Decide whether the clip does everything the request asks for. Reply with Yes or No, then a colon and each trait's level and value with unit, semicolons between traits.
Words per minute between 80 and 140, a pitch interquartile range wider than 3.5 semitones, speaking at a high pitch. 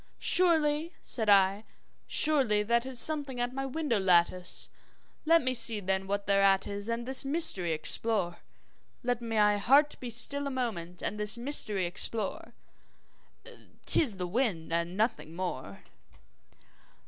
Yes: slow, 135 wpm; wide, 5.5 semitones; high, 220 Hz